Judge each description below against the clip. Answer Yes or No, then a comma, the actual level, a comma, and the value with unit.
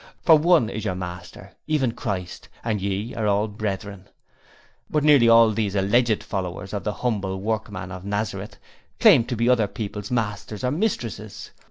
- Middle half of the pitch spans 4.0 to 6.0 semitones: No, average, 2.9 semitones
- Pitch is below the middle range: Yes, low, 105 Hz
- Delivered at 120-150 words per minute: No, average, 165 wpm